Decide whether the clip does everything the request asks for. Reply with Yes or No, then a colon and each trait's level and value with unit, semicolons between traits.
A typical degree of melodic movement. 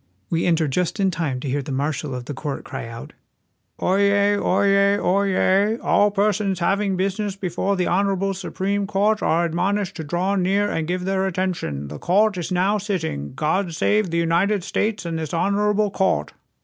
Yes: average, 3.3 semitones